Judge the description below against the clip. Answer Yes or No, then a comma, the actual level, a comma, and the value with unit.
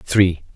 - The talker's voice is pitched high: No, very low, 90 Hz